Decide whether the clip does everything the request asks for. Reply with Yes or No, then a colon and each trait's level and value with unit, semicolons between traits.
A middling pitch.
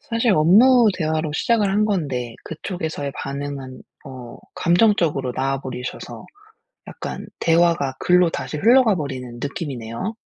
Yes: medium, 155 Hz